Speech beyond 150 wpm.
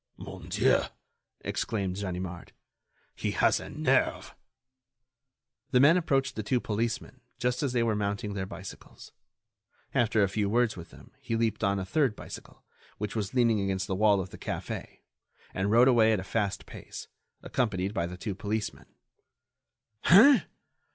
Yes: average, 160 wpm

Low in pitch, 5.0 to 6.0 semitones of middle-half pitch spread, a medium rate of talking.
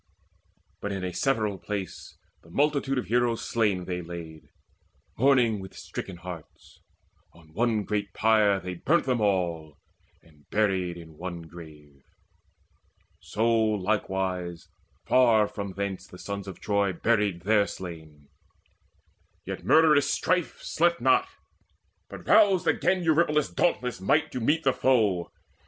No: low, 100 Hz; wide, 5.5 semitones; slow, 130 wpm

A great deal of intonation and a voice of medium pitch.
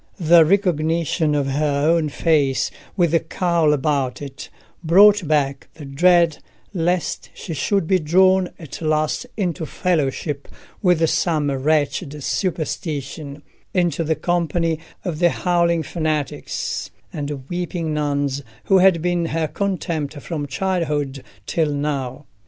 No: average, 3.2 semitones; medium, 160 Hz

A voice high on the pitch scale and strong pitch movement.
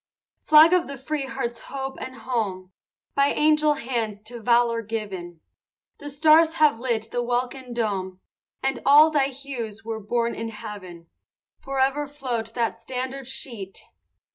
No: high, 245 Hz; average, 3.7 semitones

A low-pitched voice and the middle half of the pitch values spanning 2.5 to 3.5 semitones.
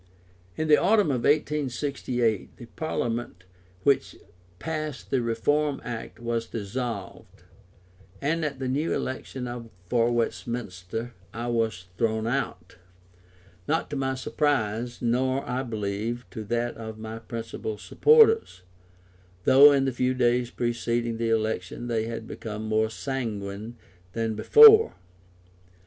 Yes: low, 120 Hz; average, 3.2 semitones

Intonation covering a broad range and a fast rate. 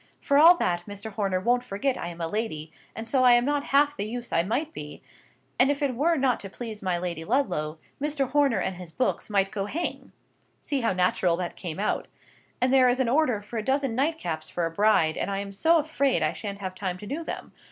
Yes: wide, 6.8 semitones; fast, 235 wpm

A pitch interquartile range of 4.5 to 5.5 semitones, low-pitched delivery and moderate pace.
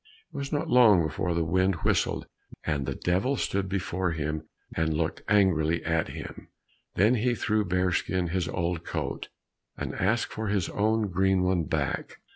No: average, 3.6 semitones; very low, 95 Hz; average, 165 wpm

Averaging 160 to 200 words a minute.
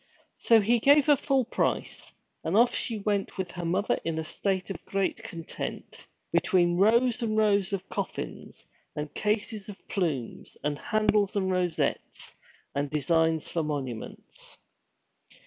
No: average, 145 wpm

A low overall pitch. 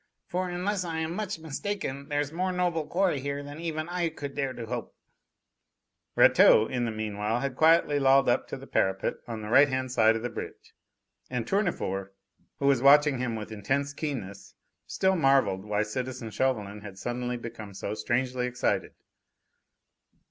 Yes: low, 130 Hz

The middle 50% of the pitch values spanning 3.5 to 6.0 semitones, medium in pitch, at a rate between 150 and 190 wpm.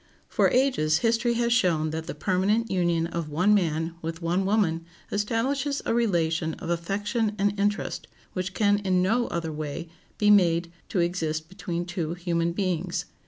Yes: average, 3.9 semitones; medium, 180 Hz; average, 165 wpm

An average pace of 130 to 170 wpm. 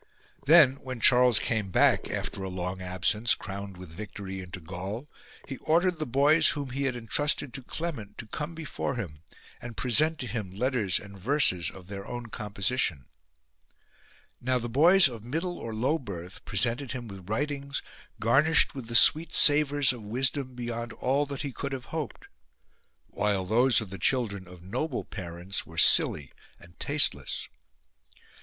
Yes: average, 165 wpm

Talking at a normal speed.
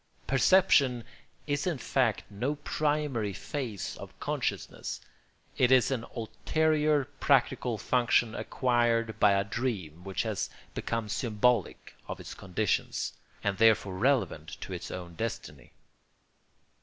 No: slow, 120 wpm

